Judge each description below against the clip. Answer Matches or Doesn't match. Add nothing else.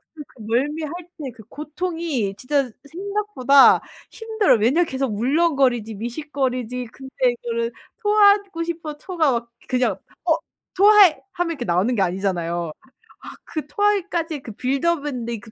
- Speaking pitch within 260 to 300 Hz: Matches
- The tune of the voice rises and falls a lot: Matches